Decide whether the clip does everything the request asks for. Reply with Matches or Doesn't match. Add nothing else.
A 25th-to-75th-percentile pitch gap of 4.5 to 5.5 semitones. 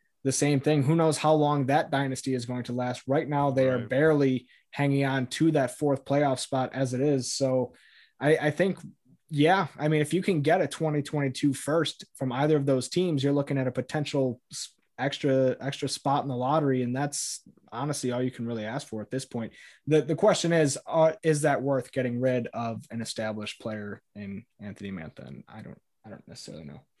Doesn't match